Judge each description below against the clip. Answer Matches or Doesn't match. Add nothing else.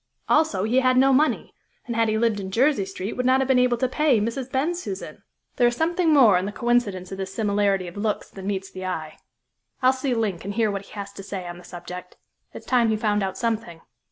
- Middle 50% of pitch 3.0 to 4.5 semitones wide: Doesn't match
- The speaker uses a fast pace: Matches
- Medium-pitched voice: Doesn't match